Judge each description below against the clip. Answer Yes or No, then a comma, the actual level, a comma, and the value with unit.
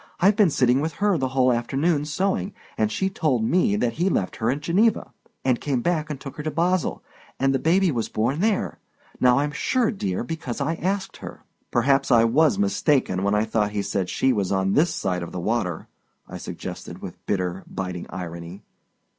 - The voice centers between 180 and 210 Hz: No, low, 135 Hz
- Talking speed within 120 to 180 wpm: No, average, 195 wpm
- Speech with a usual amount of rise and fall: No, wide, 7.8 semitones